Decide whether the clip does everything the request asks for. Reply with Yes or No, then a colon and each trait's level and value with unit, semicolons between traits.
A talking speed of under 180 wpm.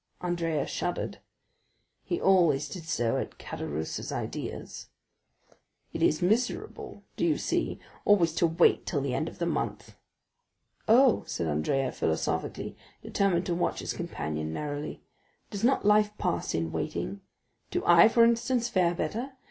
Yes: slow, 135 wpm